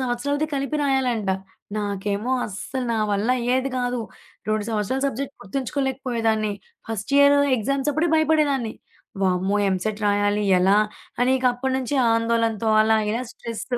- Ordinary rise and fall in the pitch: Yes, average, 4.2 semitones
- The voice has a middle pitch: No, high, 235 Hz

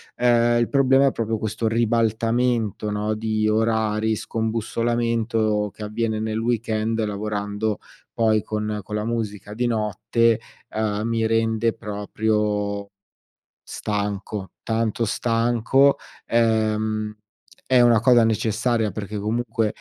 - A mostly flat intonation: Yes, narrow, 1.5 semitones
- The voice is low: Yes, low, 110 Hz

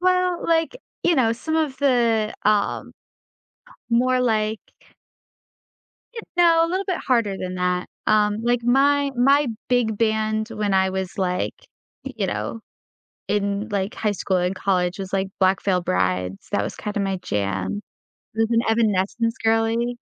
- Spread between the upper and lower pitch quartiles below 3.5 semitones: No, average, 4.5 semitones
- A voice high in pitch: Yes, high, 220 Hz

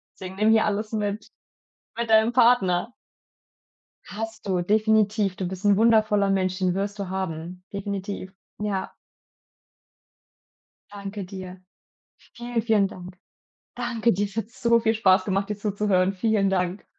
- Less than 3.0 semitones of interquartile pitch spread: Yes, narrow, 2.6 semitones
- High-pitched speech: Yes, high, 200 Hz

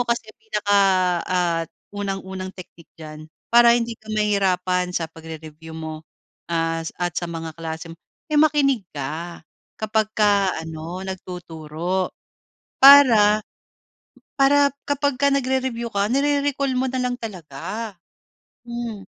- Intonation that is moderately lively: No, wide, 6.3 semitones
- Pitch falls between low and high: No, high, 195 Hz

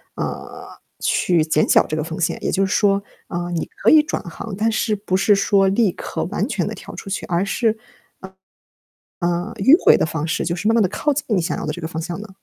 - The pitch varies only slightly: No, average, 3.8 semitones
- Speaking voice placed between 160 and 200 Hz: Yes, high, 190 Hz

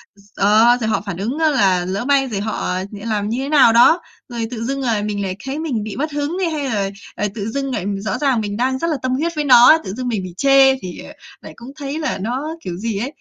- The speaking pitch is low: No, high, 240 Hz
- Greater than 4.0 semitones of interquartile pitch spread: Yes, average, 5.1 semitones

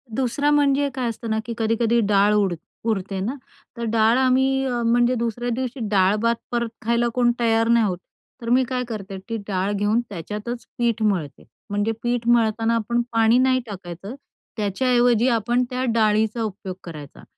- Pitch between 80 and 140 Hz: No, high, 230 Hz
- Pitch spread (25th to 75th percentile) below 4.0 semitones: Yes, narrow, 2.6 semitones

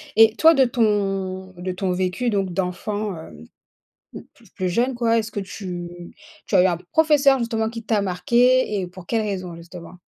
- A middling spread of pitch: Yes, average, 4.2 semitones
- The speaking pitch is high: Yes, high, 200 Hz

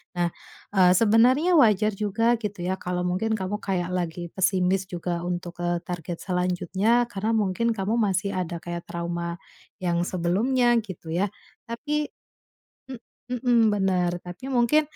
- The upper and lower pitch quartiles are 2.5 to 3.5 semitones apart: No, average, 4.1 semitones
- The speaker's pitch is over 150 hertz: Yes, high, 190 Hz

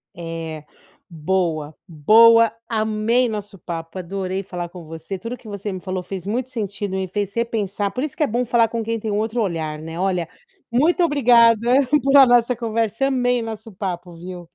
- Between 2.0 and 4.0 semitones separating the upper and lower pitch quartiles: No, average, 4.5 semitones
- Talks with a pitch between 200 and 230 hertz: Yes, high, 205 Hz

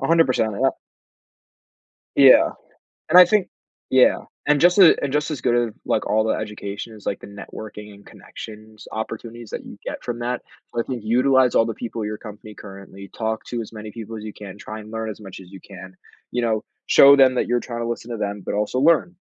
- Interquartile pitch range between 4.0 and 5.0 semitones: No, average, 2.9 semitones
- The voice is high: No, low, 110 Hz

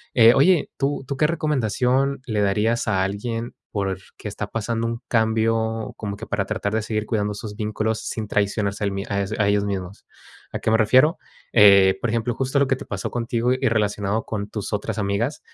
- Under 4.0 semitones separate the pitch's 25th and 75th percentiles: Yes, narrow, 2.6 semitones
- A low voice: Yes, low, 110 Hz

